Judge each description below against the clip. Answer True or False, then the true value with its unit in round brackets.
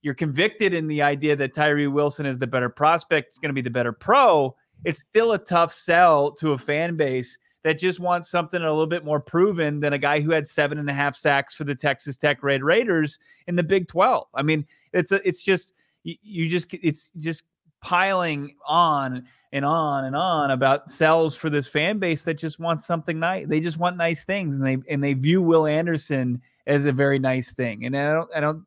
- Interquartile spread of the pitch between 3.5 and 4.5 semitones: False (3.1 semitones)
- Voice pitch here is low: False (155 Hz)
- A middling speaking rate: False (225 wpm)